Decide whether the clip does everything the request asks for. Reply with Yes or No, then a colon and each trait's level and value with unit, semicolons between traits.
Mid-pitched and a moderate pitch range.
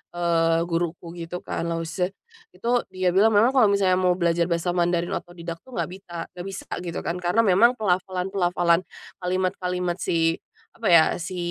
No: medium, 180 Hz; narrow, 1.8 semitones